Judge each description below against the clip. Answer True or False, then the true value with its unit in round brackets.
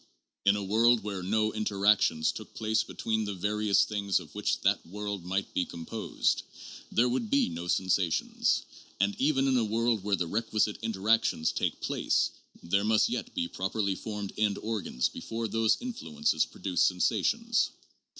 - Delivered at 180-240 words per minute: False (160 wpm)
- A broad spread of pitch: False (3.0 semitones)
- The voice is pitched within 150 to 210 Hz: False (105 Hz)